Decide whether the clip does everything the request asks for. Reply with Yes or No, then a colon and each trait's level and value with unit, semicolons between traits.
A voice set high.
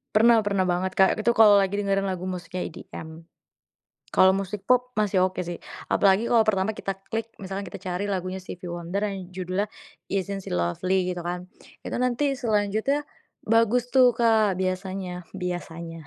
Yes: high, 195 Hz